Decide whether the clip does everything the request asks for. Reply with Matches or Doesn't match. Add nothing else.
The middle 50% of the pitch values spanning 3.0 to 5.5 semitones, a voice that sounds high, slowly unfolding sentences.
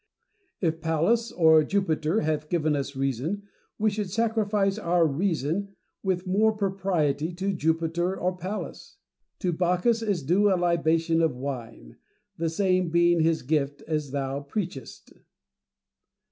Doesn't match